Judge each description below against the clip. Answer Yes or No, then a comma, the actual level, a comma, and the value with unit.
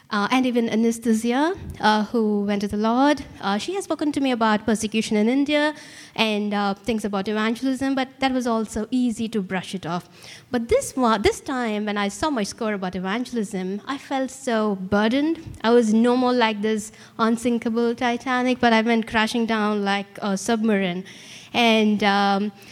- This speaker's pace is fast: No, average, 180 wpm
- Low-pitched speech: No, high, 225 Hz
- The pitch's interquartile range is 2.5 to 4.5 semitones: Yes, average, 3.2 semitones